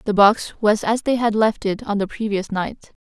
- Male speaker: No, female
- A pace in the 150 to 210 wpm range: No, fast, 240 wpm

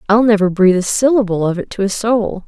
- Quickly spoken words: Yes, fast, 245 wpm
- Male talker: No, female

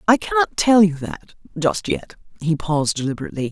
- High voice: No, medium, 170 Hz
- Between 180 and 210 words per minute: No, average, 155 wpm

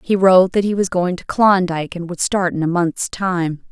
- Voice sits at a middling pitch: Yes, medium, 180 Hz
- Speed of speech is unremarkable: No, fast, 240 wpm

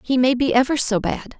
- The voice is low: No, very high, 255 Hz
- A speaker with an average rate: No, fast, 260 wpm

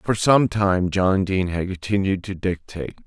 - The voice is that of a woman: No, male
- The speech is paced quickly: No, average, 175 wpm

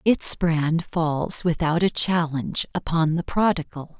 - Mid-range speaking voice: Yes, medium, 165 Hz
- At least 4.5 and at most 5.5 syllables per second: No, 3.9 syllables/s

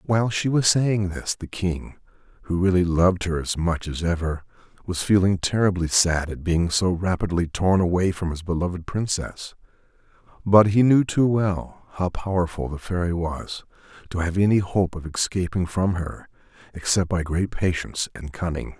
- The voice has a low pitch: Yes, very low, 90 Hz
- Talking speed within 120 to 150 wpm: No, average, 170 wpm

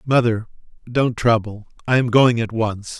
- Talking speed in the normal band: Yes, average, 160 wpm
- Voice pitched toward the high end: No, low, 115 Hz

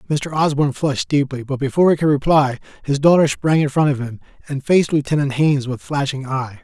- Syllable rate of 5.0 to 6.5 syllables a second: Yes, 6.1 syllables/s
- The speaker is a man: Yes, male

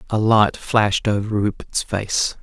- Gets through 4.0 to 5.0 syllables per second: Yes, 4.1 syllables/s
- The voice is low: Yes, low, 105 Hz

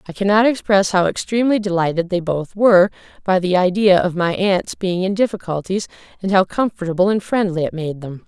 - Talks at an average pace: Yes, average, 190 wpm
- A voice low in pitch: No, high, 190 Hz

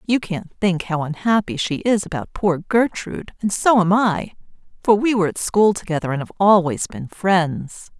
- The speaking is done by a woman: Yes, female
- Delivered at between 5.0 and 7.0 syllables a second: No, 4.8 syllables/s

